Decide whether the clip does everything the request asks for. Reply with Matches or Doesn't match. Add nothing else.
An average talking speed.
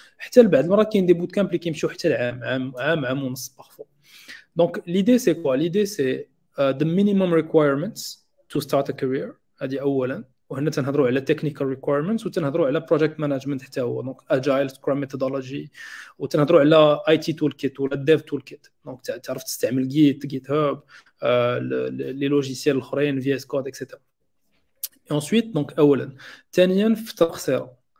Doesn't match